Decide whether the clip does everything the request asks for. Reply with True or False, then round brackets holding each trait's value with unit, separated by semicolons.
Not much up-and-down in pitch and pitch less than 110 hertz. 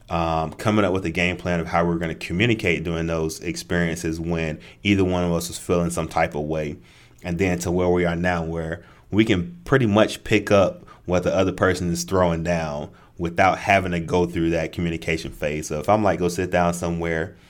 True (1.6 semitones; 85 Hz)